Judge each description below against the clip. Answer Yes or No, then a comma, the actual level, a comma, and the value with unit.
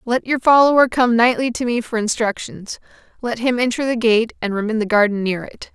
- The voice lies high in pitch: Yes, high, 235 Hz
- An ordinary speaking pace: No, fast, 220 wpm